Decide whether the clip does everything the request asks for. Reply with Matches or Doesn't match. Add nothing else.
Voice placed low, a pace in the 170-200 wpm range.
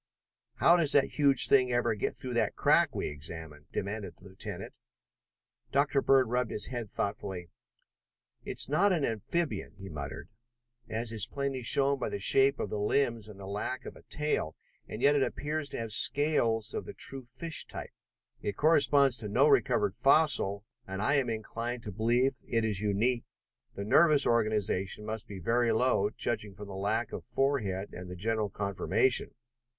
Matches